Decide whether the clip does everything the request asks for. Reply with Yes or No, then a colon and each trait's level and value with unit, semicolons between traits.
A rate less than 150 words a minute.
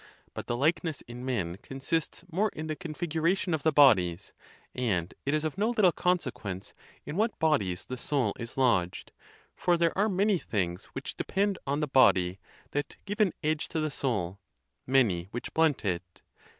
No: average, 175 wpm